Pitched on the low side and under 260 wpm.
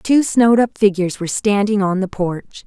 No: high, 205 Hz; fast, 205 wpm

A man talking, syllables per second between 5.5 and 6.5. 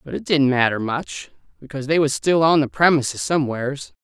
Yes: male; 5.9 syllables/s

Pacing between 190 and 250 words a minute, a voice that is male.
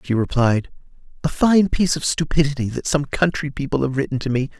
Yes: average, 195 wpm; male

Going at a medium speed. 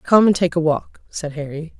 No: fast, 235 wpm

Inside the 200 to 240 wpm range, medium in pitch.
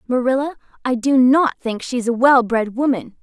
No: fast, 205 wpm; very high, 255 Hz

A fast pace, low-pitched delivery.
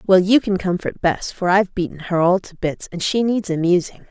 No: fast, 235 wpm; medium, 185 Hz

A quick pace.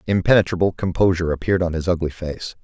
No: average, 160 wpm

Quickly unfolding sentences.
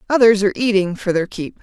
Yes: fast, 220 wpm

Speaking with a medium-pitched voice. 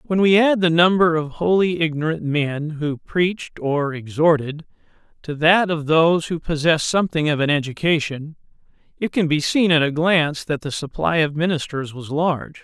Yes: medium, 160 Hz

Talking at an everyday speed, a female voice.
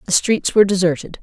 Yes: average, 195 wpm; female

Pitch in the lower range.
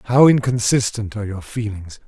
Yes: low, 115 Hz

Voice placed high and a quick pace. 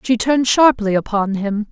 No: high, 225 Hz; average, 175 wpm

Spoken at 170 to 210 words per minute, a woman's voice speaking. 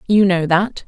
Yes: fast, 205 wpm; female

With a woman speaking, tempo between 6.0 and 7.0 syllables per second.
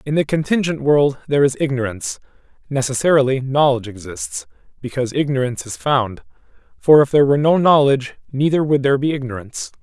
No: male; 6.5 syllables/s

